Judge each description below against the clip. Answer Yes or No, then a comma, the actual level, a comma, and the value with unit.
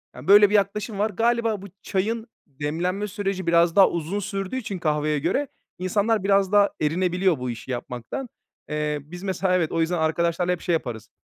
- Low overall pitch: No, medium, 185 Hz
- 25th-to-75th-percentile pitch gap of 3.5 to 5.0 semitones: Yes, average, 4.1 semitones